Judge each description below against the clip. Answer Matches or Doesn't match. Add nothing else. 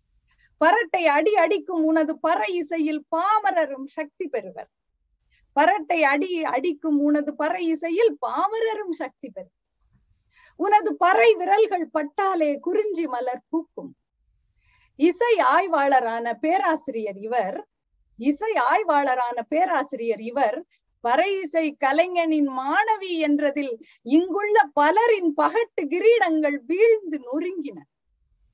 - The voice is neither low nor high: Doesn't match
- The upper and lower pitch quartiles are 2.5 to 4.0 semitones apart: Doesn't match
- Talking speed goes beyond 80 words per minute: Matches